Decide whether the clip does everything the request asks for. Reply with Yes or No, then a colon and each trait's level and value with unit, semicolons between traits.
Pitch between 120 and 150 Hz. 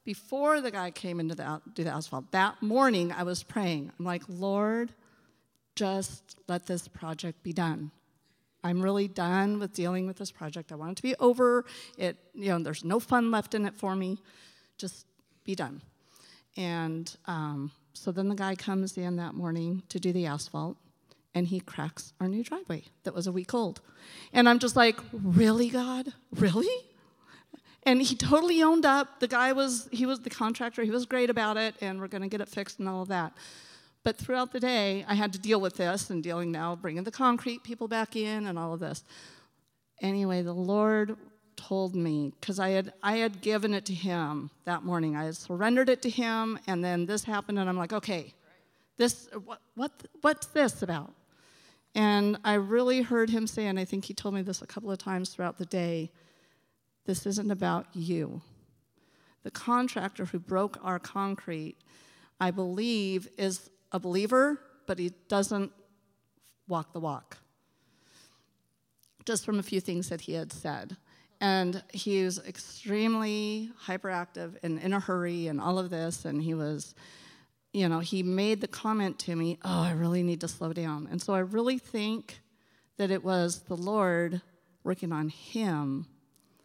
No: high, 190 Hz